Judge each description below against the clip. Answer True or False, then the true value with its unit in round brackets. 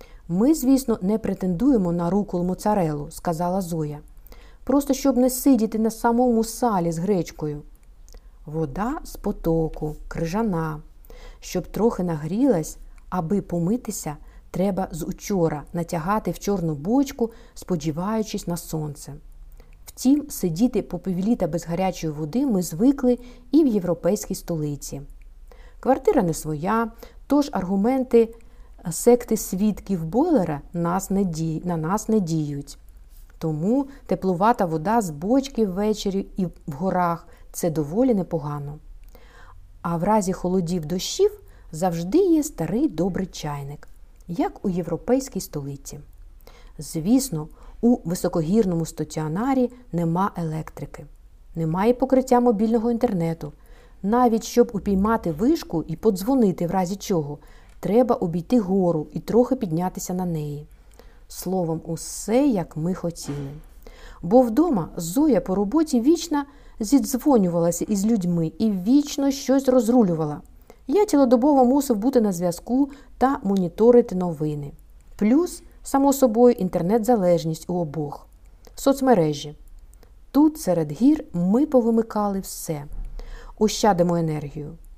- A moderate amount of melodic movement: False (6.6 semitones)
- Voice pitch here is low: False (190 Hz)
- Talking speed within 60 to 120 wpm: True (110 wpm)